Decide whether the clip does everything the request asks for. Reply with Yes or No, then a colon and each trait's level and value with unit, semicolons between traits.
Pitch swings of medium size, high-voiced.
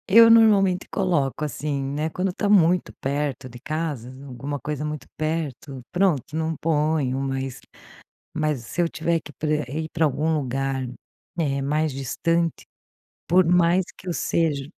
No: average, 3.6 semitones; medium, 155 Hz